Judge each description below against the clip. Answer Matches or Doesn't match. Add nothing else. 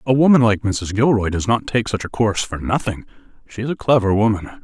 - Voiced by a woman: Doesn't match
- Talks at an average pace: Doesn't match